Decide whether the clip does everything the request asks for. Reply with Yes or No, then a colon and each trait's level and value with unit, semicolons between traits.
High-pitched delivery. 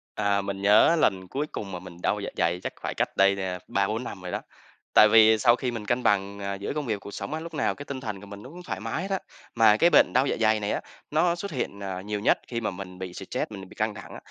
No: low, 105 Hz